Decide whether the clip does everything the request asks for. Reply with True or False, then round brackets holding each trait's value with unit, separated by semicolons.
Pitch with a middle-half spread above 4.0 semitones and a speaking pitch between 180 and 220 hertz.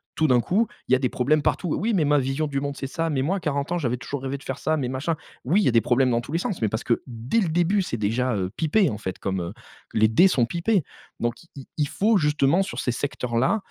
False (5.5 semitones; 140 Hz)